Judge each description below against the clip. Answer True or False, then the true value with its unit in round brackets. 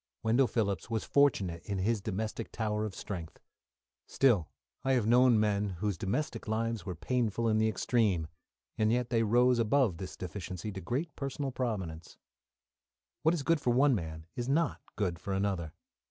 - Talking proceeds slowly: False (170 wpm)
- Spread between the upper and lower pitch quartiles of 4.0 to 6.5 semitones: True (4.3 semitones)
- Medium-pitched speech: False (110 Hz)